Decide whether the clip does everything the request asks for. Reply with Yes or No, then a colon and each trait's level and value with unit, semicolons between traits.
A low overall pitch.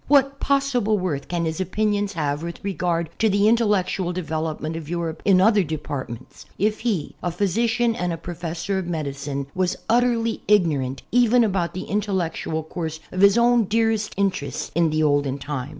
No: medium, 180 Hz